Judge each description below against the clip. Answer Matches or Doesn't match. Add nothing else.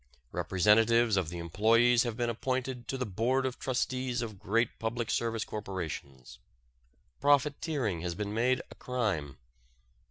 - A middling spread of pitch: Matches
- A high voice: Doesn't match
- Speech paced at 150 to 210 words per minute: Doesn't match